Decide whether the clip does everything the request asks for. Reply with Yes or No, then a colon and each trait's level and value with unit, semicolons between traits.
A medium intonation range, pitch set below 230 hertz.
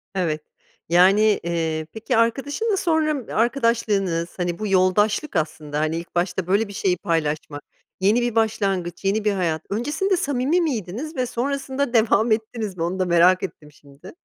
No: wide, 5.9 semitones; high, 200 Hz